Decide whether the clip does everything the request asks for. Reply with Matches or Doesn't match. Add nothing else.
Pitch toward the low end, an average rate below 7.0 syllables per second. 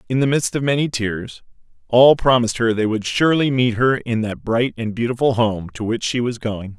Matches